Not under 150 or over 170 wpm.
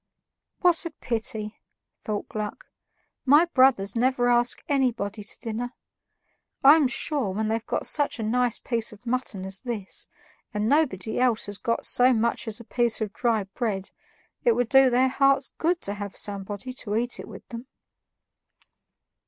Yes: average, 160 wpm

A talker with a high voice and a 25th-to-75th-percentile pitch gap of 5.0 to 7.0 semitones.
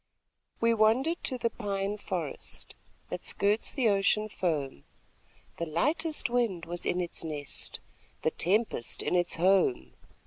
Yes: high, 195 Hz; average, 5.3 semitones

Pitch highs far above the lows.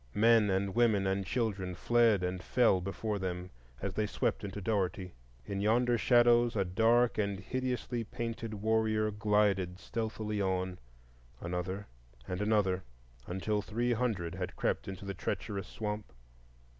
No: average, 3.2 semitones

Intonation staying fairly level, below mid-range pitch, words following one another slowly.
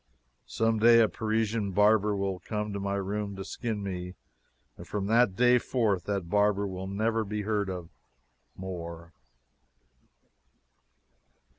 Yes: narrow, 2.3 semitones; low, 100 Hz; slow, 130 wpm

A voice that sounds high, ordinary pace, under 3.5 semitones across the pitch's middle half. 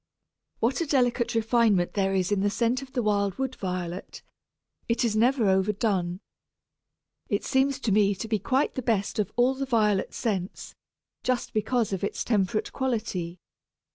No: high, 215 Hz; average, 165 wpm; average, 4.0 semitones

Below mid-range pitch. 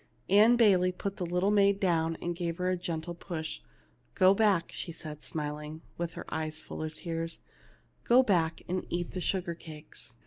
No: medium, 175 Hz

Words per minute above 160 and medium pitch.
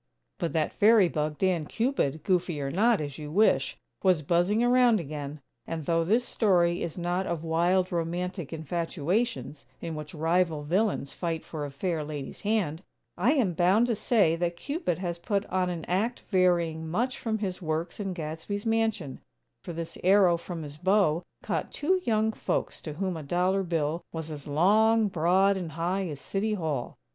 Yes: average, 175 wpm; medium, 175 Hz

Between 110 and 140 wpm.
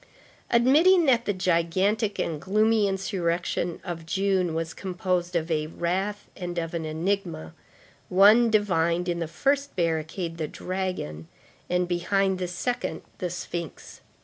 Yes: slow, 135 wpm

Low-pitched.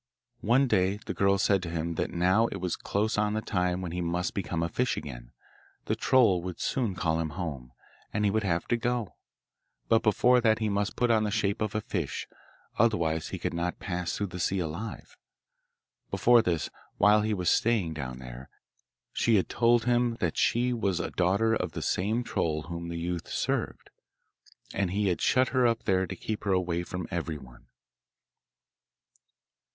Yes: very low, 95 Hz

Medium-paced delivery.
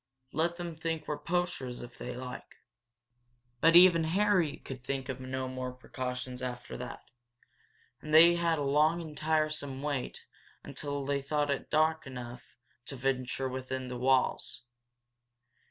Yes: average, 150 wpm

